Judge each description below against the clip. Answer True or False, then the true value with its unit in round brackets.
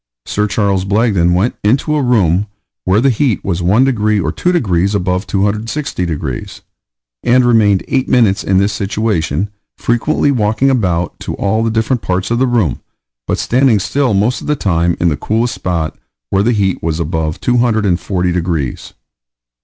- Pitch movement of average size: True (4.8 semitones)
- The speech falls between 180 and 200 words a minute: False (170 wpm)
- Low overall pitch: True (105 Hz)